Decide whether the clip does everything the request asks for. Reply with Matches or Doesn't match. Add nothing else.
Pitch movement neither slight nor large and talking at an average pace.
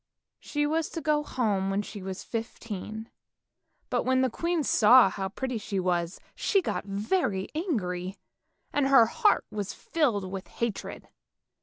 Doesn't match